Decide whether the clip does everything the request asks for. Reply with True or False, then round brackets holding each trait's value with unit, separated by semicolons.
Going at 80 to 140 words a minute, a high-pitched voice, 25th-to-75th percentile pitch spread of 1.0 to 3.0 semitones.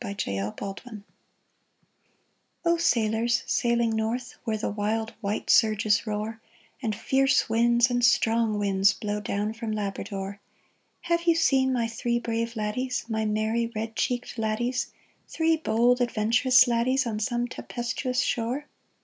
True (135 wpm; 230 Hz; 2.4 semitones)